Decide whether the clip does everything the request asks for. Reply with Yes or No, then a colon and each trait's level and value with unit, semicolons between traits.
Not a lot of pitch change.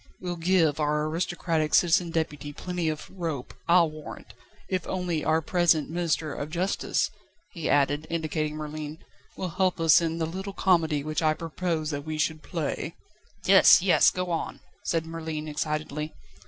Yes: narrow, 2.1 semitones